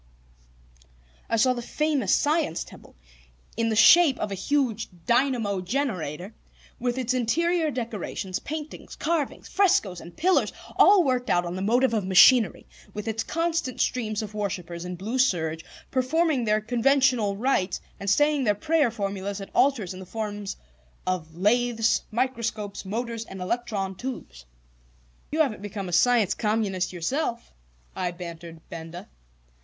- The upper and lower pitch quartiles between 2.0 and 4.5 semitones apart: No, wide, 5.4 semitones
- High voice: Yes, high, 225 Hz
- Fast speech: No, average, 145 wpm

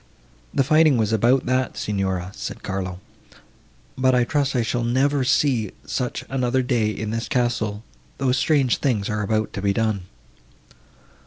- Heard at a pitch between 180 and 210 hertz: No, low, 120 Hz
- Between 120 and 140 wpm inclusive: No, average, 155 wpm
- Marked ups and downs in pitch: No, average, 3.7 semitones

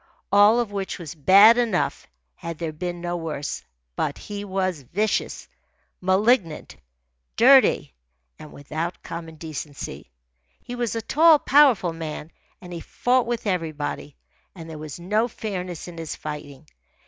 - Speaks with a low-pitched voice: No, medium, 175 Hz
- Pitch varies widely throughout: No, average, 5.0 semitones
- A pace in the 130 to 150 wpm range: Yes, average, 140 wpm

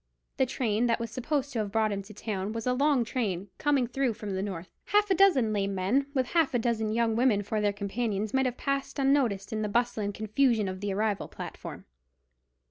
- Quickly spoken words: Yes, fast, 220 wpm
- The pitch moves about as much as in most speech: Yes, average, 4.1 semitones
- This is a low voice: No, high, 225 Hz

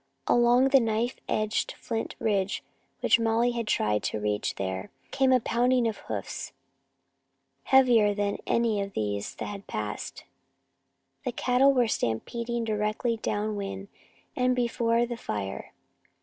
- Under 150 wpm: Yes, slow, 135 wpm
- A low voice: No, high, 225 Hz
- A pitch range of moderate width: Yes, average, 3.4 semitones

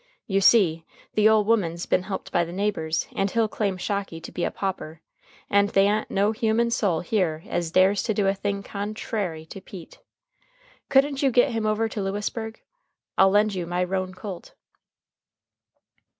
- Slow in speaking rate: No, average, 175 wpm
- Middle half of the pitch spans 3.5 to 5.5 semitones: No, average, 3.0 semitones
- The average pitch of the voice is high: Yes, high, 200 Hz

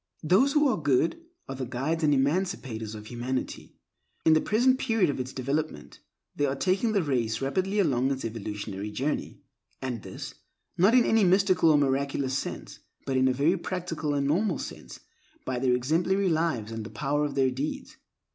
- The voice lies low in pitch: No, medium, 145 Hz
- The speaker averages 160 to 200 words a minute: Yes, average, 185 wpm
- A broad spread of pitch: Yes, wide, 5.9 semitones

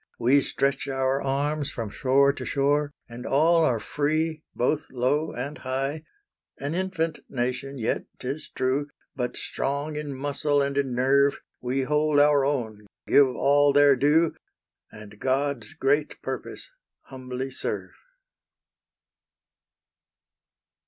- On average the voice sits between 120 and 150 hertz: Yes, medium, 140 Hz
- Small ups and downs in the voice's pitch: Yes, narrow, 2.1 semitones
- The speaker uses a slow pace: Yes, slow, 125 wpm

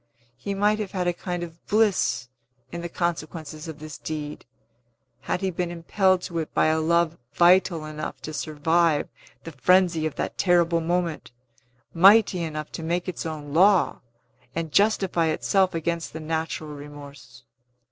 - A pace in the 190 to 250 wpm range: No, average, 155 wpm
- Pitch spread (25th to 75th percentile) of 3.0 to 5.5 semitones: No, narrow, 2.6 semitones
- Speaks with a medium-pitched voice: Yes, medium, 165 Hz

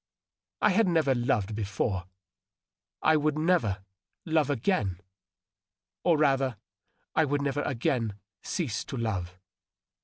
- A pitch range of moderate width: No, wide, 7.4 semitones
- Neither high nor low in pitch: No, low, 130 Hz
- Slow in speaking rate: Yes, slow, 120 wpm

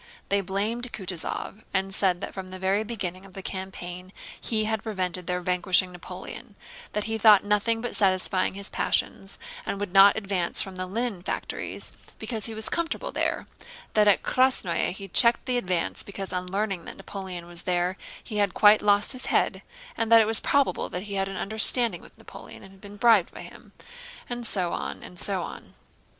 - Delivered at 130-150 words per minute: No, average, 195 wpm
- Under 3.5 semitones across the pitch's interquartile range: Yes, average, 2.9 semitones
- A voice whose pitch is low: No, high, 195 Hz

